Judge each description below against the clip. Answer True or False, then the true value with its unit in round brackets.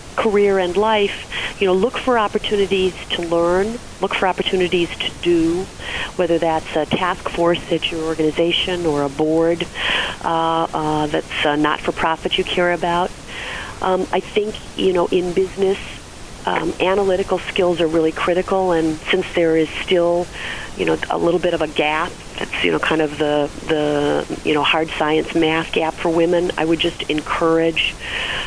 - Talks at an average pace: True (160 wpm)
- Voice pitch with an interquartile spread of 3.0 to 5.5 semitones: False (2.6 semitones)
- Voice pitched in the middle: True (170 Hz)